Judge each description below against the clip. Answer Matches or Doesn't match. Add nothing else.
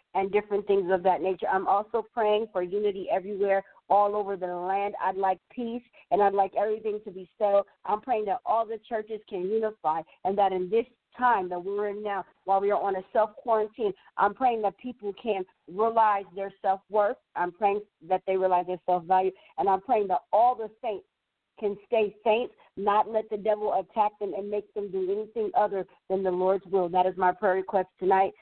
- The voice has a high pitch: Matches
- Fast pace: Matches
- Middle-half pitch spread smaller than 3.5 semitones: Matches